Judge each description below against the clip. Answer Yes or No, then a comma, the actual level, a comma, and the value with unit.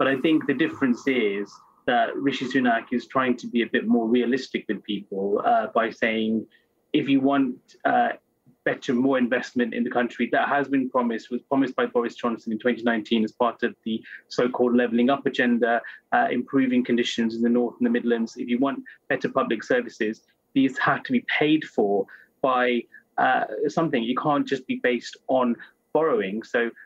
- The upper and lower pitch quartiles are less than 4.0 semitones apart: Yes, narrow, 2.5 semitones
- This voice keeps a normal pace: Yes, average, 185 wpm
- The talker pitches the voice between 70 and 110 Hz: No, low, 125 Hz